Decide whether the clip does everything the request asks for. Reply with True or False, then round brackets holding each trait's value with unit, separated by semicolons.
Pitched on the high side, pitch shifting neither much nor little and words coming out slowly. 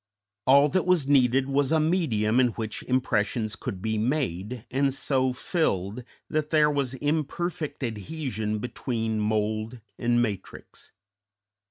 False (125 Hz; 4.8 semitones; 130 wpm)